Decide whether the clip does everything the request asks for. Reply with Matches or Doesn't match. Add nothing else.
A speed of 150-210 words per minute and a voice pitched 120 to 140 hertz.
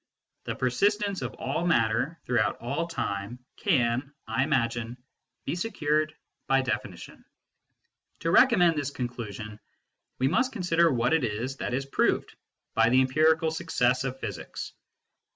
Doesn't match